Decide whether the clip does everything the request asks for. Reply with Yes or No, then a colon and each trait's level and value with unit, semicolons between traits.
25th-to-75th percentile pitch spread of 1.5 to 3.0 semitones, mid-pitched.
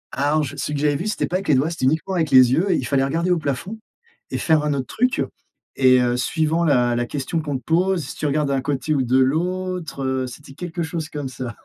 No: average, 4.1 semitones; medium, 150 Hz